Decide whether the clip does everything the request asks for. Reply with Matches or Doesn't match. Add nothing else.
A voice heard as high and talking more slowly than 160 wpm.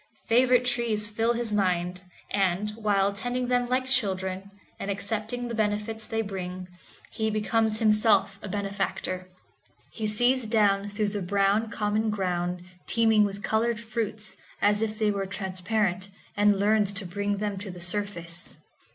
Matches